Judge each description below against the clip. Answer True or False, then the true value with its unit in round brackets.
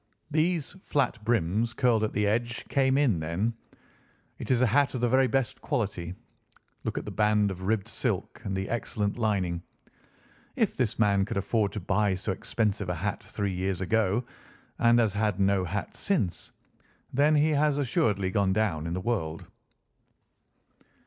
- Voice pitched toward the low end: True (105 Hz)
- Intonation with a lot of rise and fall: False (4.0 semitones)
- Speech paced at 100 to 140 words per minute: False (170 wpm)